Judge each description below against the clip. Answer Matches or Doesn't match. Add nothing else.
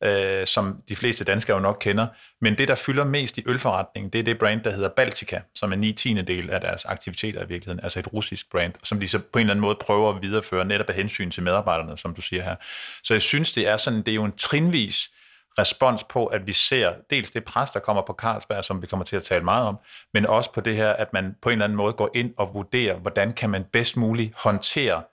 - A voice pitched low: Matches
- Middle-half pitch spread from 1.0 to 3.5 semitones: Matches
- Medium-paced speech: Doesn't match